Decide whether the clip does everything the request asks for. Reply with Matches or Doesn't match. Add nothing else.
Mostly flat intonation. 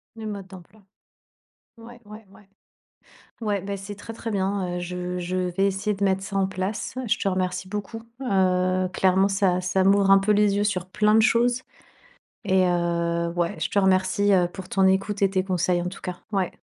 Matches